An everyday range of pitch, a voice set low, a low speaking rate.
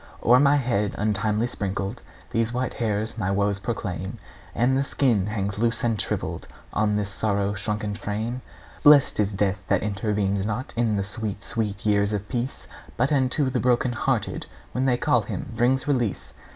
No: average, 3.2 semitones; low, 110 Hz; average, 170 wpm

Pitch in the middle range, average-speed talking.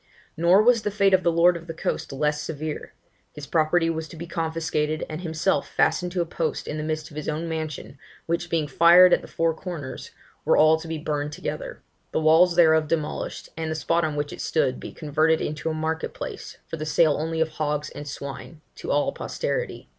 No: medium, 160 Hz; fast, 215 wpm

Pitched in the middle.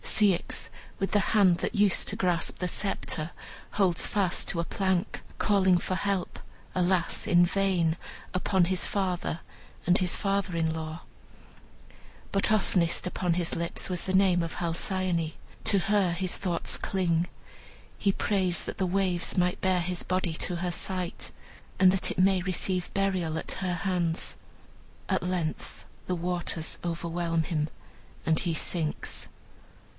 Yes: medium, 180 Hz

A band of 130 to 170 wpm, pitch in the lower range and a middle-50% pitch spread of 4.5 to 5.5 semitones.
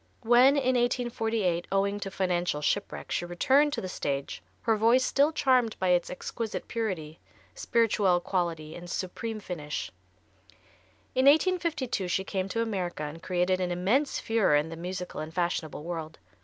No: average, 155 wpm; high, 190 Hz; average, 5.1 semitones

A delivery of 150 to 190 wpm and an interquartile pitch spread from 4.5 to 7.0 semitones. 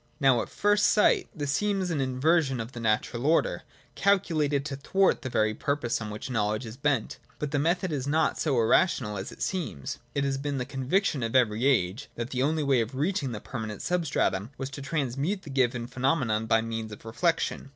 No: fast, 205 wpm; average, 4.9 semitones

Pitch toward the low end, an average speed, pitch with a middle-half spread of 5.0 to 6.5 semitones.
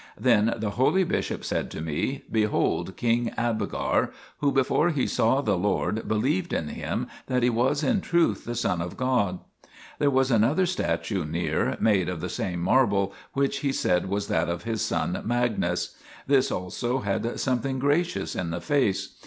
Yes: low, 115 Hz; average, 175 wpm; wide, 5.4 semitones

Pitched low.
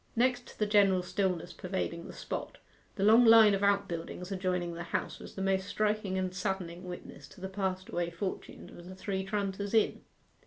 No: high, 190 Hz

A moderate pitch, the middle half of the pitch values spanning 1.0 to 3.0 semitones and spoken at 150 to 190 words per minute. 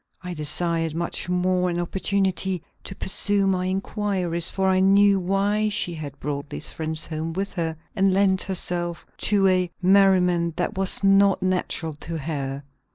Yes: medium, 180 Hz; narrow, 2.6 semitones; average, 160 wpm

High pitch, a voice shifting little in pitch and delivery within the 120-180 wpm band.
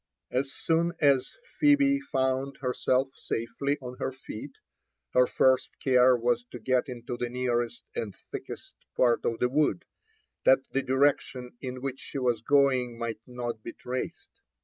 No: low, 125 Hz; narrow, 2.0 semitones; average, 150 wpm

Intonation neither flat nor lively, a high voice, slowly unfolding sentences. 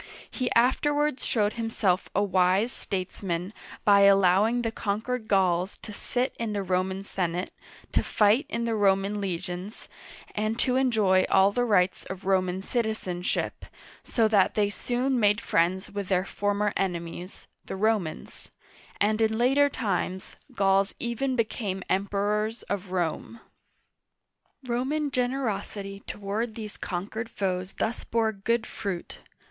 Yes: average, 3.3 semitones; high, 205 Hz; slow, 130 wpm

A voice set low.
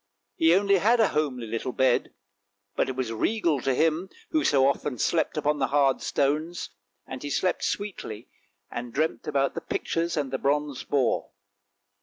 No: medium, 145 Hz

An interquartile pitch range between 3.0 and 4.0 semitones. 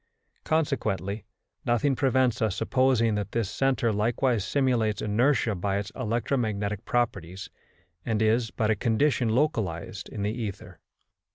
Yes: average, 3.6 semitones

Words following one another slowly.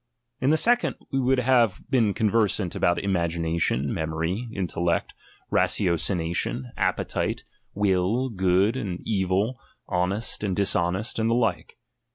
Yes: slow, 120 wpm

